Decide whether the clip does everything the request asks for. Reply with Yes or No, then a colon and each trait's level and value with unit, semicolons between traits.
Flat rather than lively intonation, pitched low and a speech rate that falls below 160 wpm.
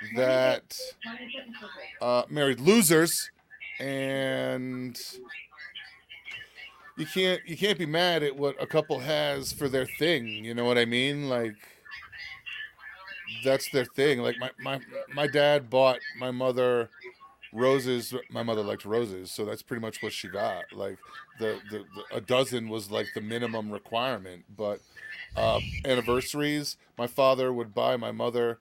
No: average, 3.7 semitones; low, 130 Hz; average, 145 wpm